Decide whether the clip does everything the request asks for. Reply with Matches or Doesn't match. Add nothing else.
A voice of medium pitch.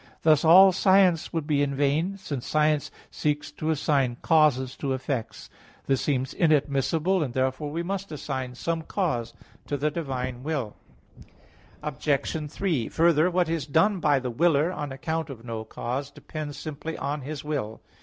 Matches